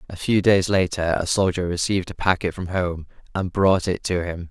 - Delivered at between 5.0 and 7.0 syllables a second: Yes, 5.2 syllables/s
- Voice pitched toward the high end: No, very low, 90 Hz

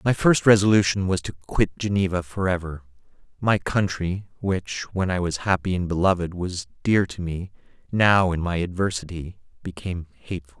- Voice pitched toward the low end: Yes, very low, 90 Hz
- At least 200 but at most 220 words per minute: No, average, 155 wpm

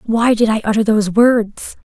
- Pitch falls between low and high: No, high, 220 Hz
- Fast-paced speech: No, average, 190 wpm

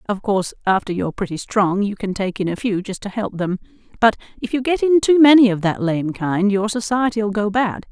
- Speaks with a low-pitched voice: No, high, 210 Hz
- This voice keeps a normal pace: No, fast, 235 wpm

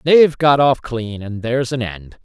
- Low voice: Yes, low, 125 Hz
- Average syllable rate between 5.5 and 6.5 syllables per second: No, 4.7 syllables/s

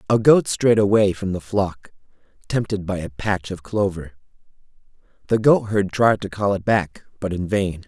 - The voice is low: Yes, low, 100 Hz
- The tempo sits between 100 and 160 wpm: No, average, 175 wpm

